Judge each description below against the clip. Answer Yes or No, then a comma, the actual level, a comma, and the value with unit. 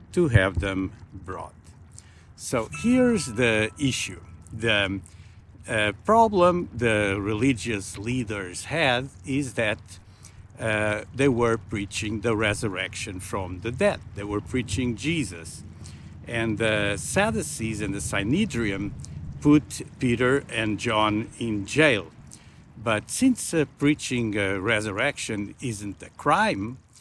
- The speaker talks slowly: Yes, slow, 115 wpm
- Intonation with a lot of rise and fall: No, average, 4.1 semitones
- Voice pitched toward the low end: Yes, low, 110 Hz